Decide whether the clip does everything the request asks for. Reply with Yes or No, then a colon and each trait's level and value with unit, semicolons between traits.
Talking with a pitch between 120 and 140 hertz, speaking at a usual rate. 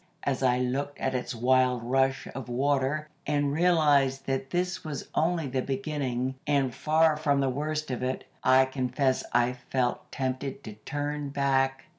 Yes: low, 135 Hz; average, 160 wpm